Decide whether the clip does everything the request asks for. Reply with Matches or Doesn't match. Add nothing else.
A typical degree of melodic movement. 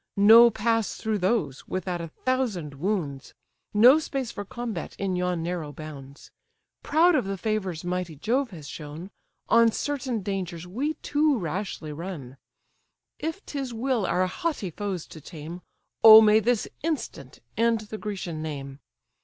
Doesn't match